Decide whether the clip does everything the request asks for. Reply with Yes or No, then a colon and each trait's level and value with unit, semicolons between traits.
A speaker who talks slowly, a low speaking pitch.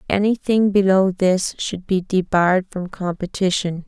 No: slow, 125 wpm; medium, 185 Hz